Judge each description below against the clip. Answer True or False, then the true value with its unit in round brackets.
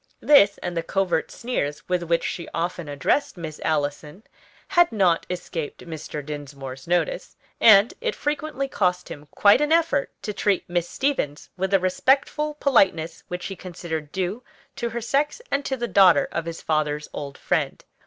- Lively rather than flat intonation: True (7.1 semitones)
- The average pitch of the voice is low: False (180 Hz)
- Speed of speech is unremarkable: True (165 wpm)